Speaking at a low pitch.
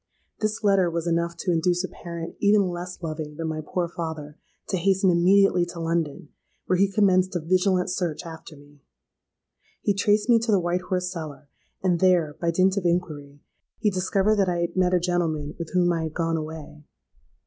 No: medium, 175 Hz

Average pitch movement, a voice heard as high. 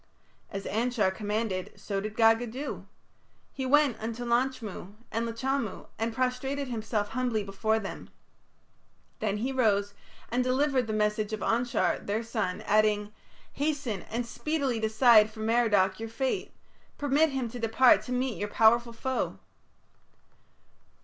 Yes: average, 3.1 semitones; high, 230 Hz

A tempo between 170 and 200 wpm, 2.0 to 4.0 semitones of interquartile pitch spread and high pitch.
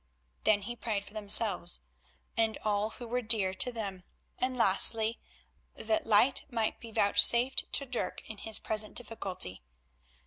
No: average, 145 wpm; narrow, 2.4 semitones; high, 220 Hz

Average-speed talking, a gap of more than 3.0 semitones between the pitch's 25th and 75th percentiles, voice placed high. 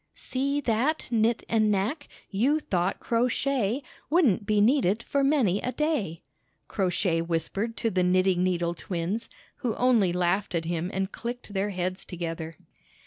Yes: average, 155 wpm; wide, 5.4 semitones; high, 205 Hz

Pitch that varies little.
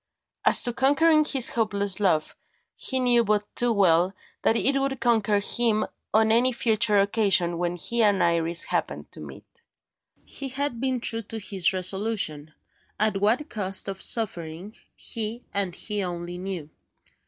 No: average, 4.1 semitones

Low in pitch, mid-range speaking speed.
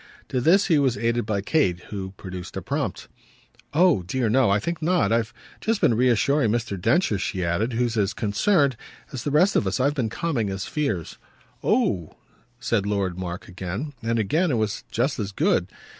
Yes: low, 115 Hz; average, 190 wpm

